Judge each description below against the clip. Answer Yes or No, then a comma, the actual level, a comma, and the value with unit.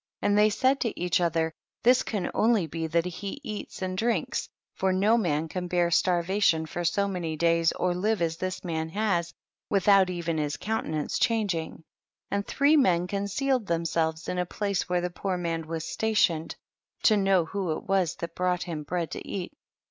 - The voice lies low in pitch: No, medium, 180 Hz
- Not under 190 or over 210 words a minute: Yes, average, 195 wpm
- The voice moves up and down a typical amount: Yes, average, 3.4 semitones